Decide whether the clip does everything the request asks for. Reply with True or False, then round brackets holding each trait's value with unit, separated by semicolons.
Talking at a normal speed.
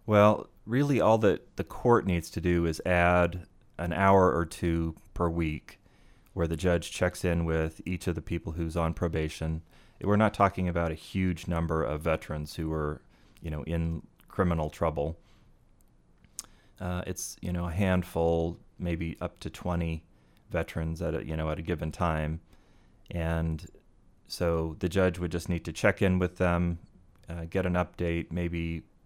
True (170 wpm)